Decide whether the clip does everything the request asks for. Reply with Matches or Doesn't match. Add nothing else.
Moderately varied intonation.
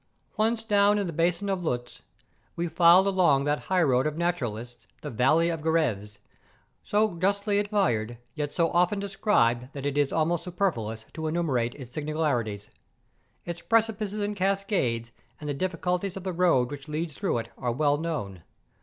Doesn't match